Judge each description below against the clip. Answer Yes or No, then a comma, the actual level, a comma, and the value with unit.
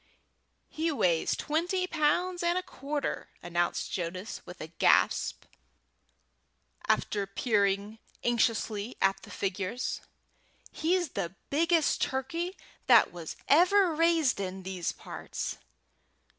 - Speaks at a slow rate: Yes, slow, 105 wpm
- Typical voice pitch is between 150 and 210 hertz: No, very high, 250 Hz